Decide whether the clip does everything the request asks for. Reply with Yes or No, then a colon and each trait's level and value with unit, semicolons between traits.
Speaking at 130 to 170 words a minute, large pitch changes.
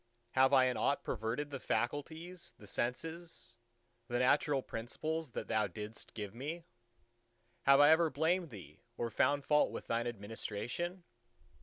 Yes: average, 145 wpm; wide, 5.7 semitones